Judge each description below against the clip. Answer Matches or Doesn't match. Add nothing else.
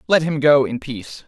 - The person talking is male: Matches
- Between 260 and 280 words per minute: Doesn't match